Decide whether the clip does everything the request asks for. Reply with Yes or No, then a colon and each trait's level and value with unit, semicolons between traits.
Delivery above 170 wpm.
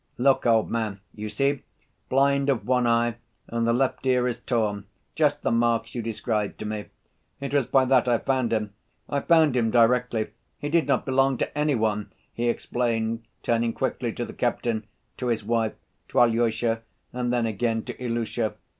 Yes: average, 180 wpm